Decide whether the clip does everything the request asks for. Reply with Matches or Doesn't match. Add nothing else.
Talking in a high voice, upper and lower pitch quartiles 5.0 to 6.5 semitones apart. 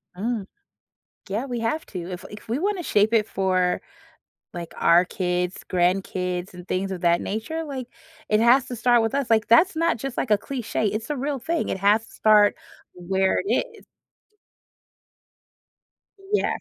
Matches